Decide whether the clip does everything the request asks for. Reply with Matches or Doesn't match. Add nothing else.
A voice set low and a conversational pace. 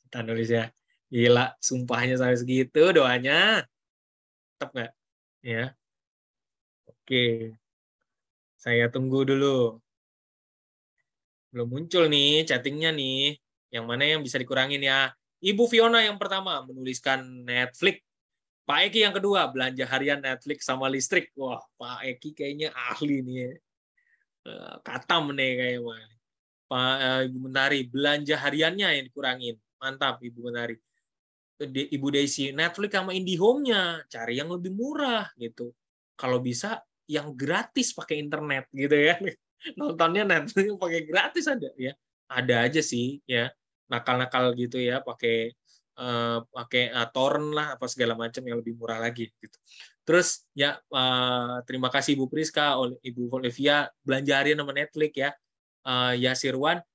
Matches